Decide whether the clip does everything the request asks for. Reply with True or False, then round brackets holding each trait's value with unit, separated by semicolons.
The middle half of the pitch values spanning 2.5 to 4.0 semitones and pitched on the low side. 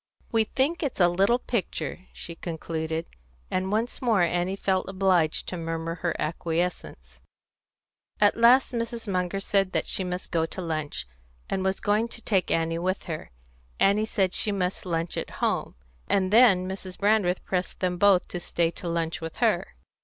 False (3.3 semitones; 185 Hz)